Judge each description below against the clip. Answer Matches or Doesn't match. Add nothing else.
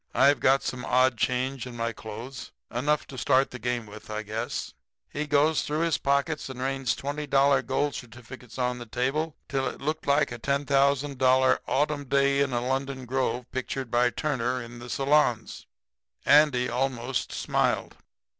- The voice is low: Matches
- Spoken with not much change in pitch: Matches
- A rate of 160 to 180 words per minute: Matches